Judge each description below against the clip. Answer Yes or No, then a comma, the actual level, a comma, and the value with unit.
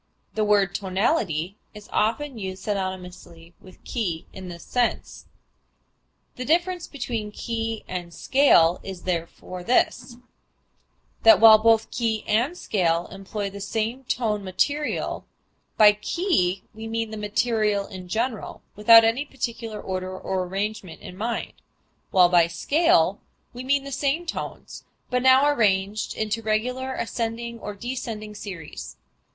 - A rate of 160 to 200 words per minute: No, slow, 135 wpm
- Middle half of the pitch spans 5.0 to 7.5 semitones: No, average, 4.2 semitones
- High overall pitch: Yes, high, 215 Hz